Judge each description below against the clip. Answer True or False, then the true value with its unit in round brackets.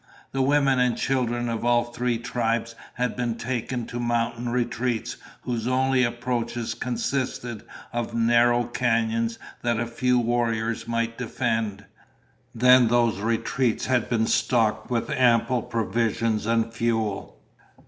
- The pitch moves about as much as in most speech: False (1.3 semitones)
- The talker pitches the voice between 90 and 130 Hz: True (120 Hz)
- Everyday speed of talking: False (130 wpm)